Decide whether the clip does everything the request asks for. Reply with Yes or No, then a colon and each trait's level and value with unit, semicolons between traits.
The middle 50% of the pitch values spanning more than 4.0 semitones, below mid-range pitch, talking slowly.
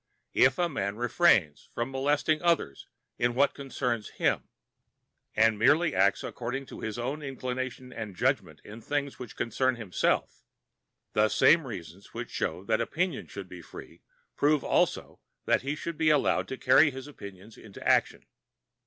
No: average, 4.9 semitones; low, 125 Hz; average, 155 wpm